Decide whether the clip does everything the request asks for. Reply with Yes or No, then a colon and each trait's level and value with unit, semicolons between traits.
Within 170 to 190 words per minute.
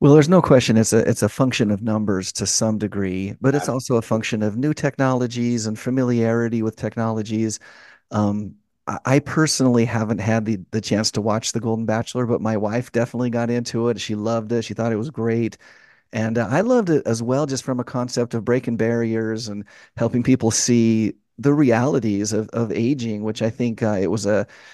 No: fast, 205 wpm